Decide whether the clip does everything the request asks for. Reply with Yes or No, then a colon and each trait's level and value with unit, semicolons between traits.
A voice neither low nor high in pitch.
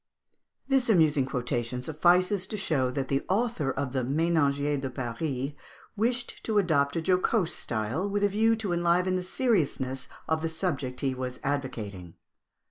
Yes: medium, 155 Hz